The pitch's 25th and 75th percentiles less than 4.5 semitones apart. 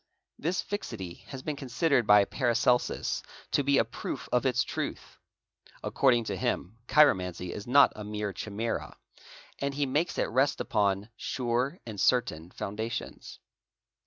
No: average, 5.0 semitones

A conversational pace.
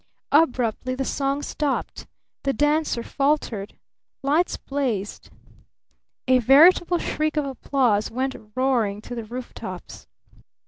No: slow, 110 wpm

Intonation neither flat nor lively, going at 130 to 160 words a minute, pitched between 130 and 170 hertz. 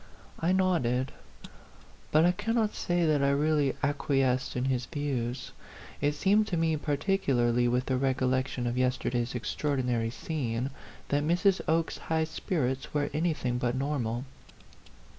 Yes: average, 4.2 semitones; average, 140 wpm; medium, 140 Hz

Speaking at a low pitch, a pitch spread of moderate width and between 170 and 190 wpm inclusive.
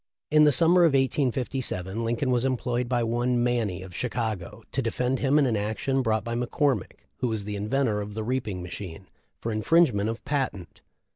Yes: low, 120 Hz; average, 3.9 semitones; average, 180 wpm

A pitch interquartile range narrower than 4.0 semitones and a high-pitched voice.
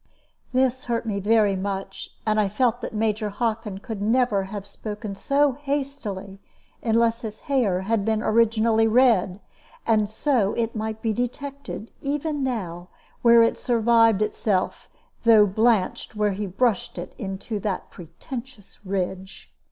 Yes: average, 3.0 semitones; high, 220 Hz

